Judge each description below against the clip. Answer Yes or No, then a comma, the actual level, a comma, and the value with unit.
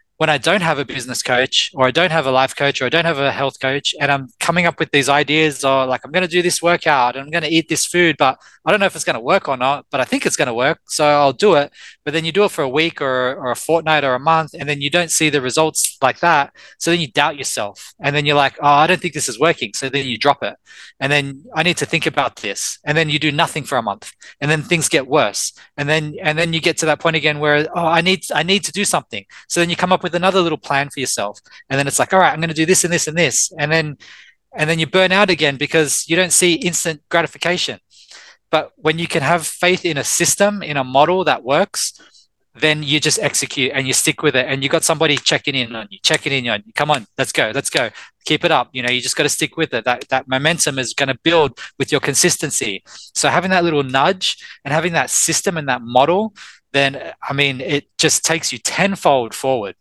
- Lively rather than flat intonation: No, average, 3.5 semitones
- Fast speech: Yes, fast, 270 wpm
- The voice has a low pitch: No, medium, 155 Hz